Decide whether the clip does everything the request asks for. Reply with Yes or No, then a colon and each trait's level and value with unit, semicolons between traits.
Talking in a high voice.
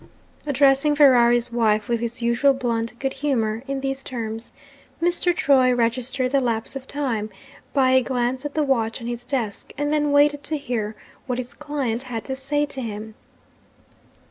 Yes: very high, 255 Hz